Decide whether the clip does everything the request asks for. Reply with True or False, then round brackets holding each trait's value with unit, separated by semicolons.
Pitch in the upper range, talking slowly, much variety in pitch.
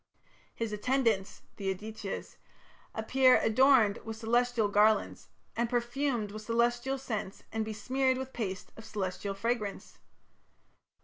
False (225 Hz; 115 wpm; 2.9 semitones)